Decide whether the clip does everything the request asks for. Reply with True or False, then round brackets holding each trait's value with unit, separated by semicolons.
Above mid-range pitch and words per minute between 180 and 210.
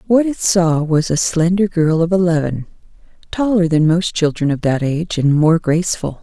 False (170 Hz; 185 wpm)